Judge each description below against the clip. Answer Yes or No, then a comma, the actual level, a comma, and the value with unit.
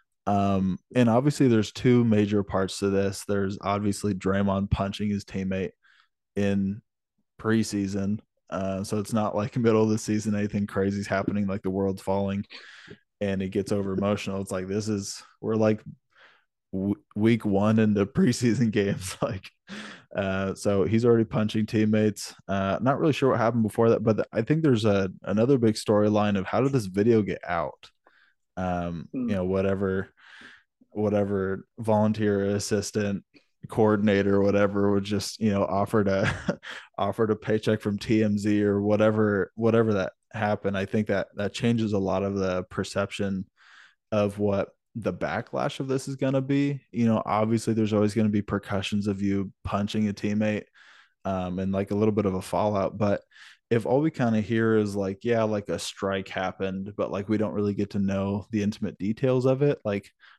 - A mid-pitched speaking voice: No, low, 105 Hz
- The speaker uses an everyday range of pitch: No, narrow, 1.9 semitones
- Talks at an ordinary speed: Yes, average, 175 wpm